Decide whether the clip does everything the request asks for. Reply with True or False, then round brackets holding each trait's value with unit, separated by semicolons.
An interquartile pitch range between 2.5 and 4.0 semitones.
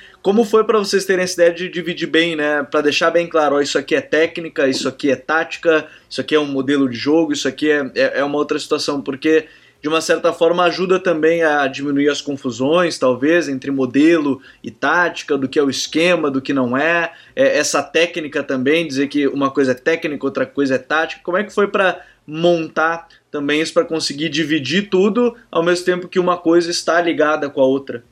True (3.2 semitones)